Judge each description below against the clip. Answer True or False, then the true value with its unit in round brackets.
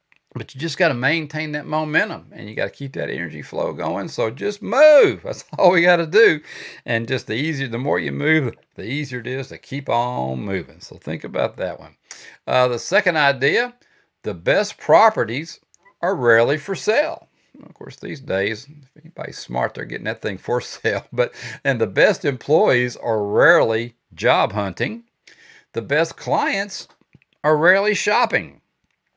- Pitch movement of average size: False (7.6 semitones)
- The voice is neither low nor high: True (150 Hz)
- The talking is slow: False (175 wpm)